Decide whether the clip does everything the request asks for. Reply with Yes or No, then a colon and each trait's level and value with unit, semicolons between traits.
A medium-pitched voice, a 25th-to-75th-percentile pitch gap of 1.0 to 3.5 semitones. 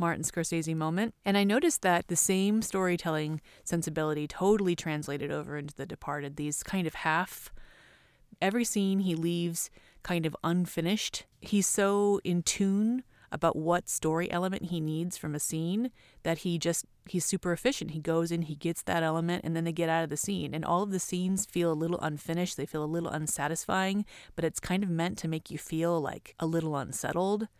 Yes: medium, 170 Hz; average, 3.2 semitones